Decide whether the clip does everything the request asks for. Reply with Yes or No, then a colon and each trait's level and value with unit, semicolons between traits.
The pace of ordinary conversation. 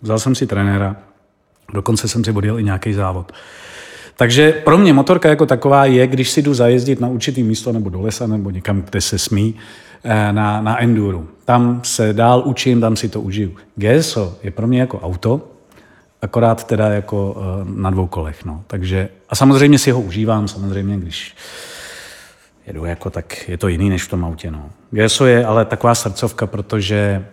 No: fast, 180 wpm